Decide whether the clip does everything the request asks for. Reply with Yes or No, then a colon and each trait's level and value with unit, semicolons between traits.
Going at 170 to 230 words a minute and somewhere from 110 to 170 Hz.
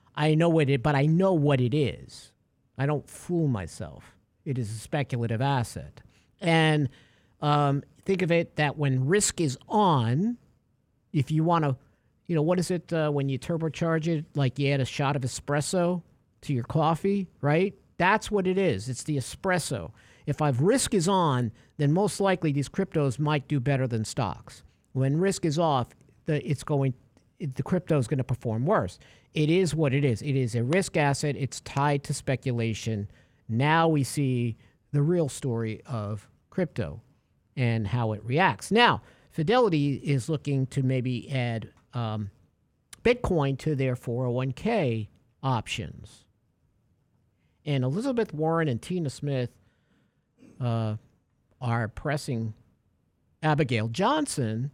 No: average, 155 wpm; medium, 140 Hz